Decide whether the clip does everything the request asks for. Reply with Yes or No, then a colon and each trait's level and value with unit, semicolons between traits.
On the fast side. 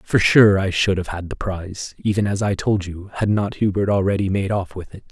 Yes: fast, 245 wpm